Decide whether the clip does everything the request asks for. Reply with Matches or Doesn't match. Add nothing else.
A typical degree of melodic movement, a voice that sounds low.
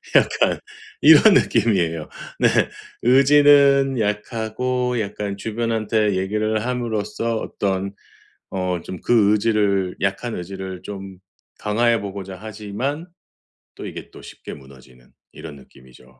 Matches